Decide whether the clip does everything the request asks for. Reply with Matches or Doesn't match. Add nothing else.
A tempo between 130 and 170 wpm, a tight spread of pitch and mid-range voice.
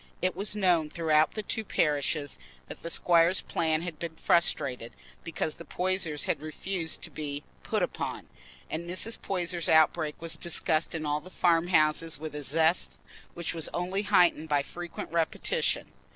Matches